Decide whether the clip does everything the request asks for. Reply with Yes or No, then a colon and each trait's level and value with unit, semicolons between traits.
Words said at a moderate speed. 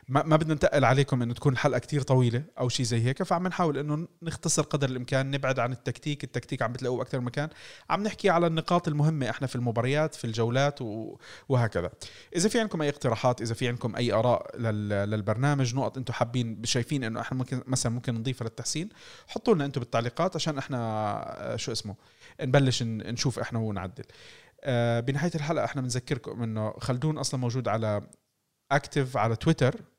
No: fast, 170 wpm